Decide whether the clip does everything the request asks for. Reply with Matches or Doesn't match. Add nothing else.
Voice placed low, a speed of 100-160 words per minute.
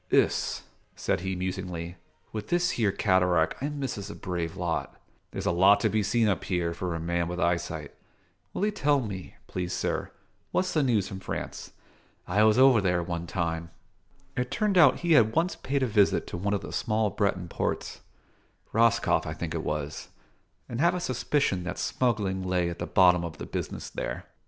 Doesn't match